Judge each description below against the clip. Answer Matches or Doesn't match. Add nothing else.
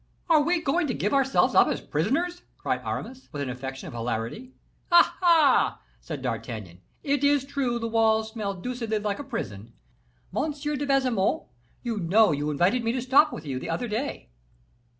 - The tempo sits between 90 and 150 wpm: Doesn't match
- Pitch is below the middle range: Doesn't match